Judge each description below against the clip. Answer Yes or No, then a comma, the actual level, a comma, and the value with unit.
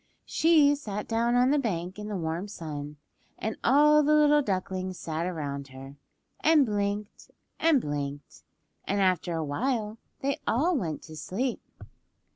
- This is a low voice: No, high, 205 Hz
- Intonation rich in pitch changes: Yes, wide, 8.7 semitones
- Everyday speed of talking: Yes, average, 150 wpm